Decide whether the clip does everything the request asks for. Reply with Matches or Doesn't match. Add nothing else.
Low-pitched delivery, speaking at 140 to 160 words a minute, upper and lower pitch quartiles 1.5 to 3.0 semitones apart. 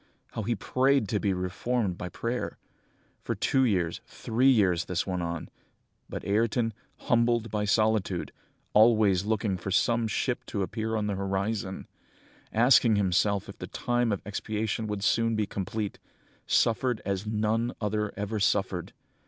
Matches